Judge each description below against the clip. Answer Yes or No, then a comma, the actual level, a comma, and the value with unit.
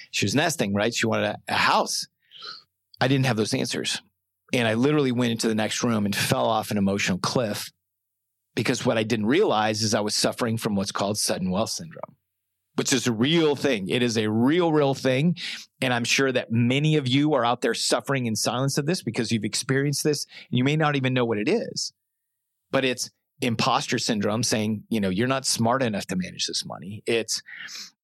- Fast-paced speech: Yes, fast, 210 wpm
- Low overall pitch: Yes, low, 120 Hz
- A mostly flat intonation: No, average, 3.8 semitones